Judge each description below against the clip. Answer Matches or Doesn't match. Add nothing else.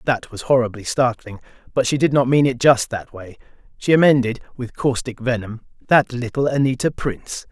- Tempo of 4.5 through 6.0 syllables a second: Matches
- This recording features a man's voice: Matches